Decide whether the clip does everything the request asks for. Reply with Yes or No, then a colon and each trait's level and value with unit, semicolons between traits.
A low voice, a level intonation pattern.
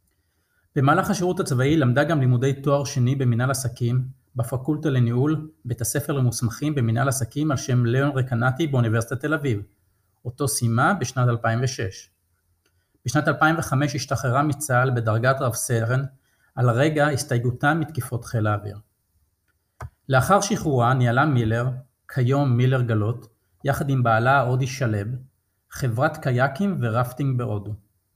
No: low, 125 Hz; average, 3.4 semitones